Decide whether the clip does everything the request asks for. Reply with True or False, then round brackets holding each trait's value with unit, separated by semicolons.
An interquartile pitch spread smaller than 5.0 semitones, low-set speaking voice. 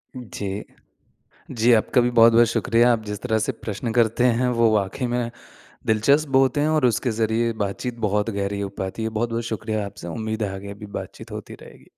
True (2.7 semitones; 115 Hz)